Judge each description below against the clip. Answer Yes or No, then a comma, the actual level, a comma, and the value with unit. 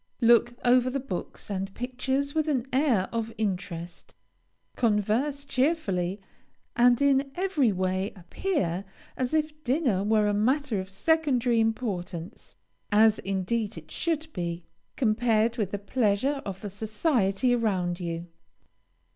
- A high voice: Yes, high, 225 Hz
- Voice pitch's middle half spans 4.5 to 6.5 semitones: Yes, average, 5.3 semitones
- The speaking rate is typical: No, slow, 130 wpm